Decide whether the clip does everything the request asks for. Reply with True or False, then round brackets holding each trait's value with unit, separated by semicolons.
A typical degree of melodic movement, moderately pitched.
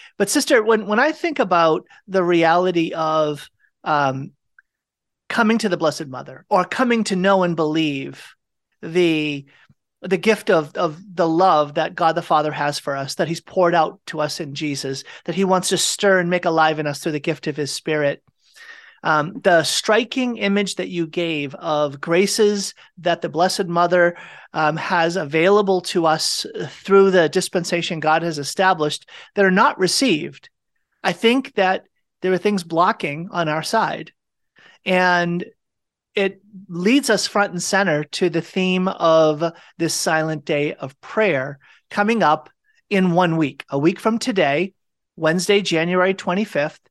True (3.6 semitones; 175 Hz)